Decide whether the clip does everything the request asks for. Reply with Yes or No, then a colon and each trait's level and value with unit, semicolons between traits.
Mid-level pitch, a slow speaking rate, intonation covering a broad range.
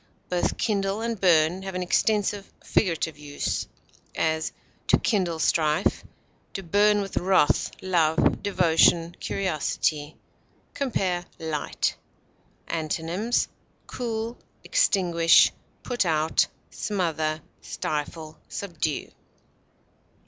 No: medium, 175 Hz; slow, 90 wpm; average, 4.0 semitones